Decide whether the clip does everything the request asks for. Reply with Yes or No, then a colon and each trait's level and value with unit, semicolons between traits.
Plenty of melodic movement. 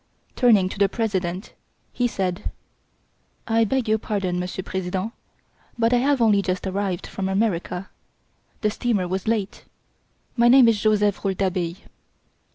No: average, 3.4 semitones